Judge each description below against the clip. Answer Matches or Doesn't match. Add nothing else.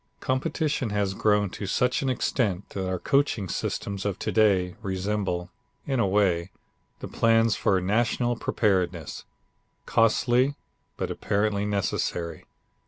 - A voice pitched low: Matches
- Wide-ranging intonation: Doesn't match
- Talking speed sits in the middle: Doesn't match